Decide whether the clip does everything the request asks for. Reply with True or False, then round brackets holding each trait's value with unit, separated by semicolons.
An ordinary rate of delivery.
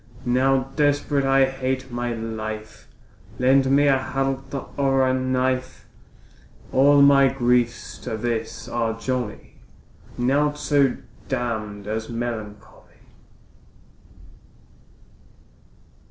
False (95 wpm)